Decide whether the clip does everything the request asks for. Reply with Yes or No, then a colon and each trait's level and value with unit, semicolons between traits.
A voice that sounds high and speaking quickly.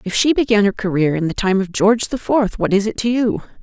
Yes: high, 210 Hz; fast, 280 wpm